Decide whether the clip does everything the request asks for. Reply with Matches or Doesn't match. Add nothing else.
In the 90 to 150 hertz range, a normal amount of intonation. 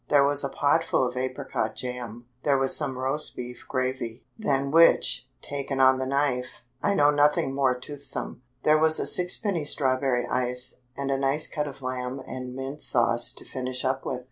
Doesn't match